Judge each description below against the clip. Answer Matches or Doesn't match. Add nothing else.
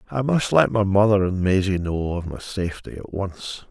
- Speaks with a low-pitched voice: Matches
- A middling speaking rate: Matches